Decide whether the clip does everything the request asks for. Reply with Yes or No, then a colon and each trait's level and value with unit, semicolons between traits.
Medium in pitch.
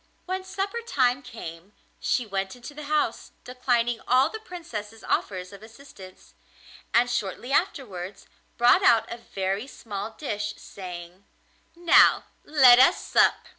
No: high, 235 Hz